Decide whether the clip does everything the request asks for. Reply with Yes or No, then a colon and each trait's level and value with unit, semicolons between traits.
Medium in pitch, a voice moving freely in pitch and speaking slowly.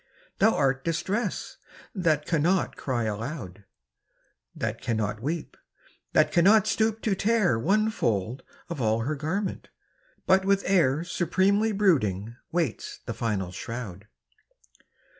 Yes: medium, 155 Hz; wide, 9.0 semitones; slow, 120 wpm